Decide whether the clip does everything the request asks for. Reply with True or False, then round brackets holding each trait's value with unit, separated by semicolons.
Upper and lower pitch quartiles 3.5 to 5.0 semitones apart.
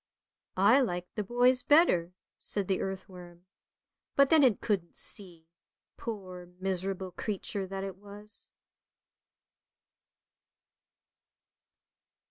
False (2.9 semitones)